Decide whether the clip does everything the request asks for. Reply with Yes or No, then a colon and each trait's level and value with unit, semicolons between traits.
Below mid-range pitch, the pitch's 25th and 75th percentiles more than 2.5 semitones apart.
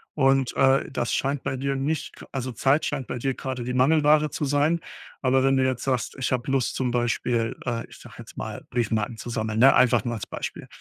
No: low, 130 Hz; narrow, 2.1 semitones